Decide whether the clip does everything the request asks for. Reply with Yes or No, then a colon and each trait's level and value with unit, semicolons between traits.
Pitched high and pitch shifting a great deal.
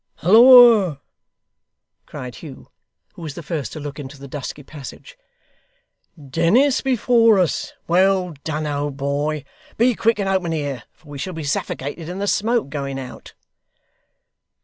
No: medium, 160 Hz; wide, 6.0 semitones